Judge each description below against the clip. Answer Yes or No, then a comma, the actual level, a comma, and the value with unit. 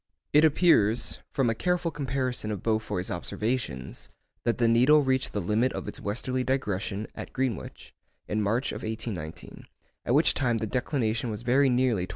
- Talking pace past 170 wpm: No, average, 165 wpm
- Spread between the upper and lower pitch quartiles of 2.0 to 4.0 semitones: Yes, average, 3.6 semitones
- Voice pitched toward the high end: No, low, 120 Hz